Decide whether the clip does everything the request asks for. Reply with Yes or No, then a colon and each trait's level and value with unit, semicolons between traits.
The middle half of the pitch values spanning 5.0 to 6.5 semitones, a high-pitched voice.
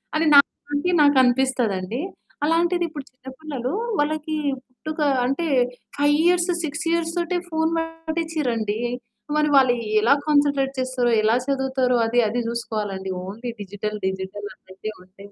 Yes: wide, 5.5 semitones; very high, 265 Hz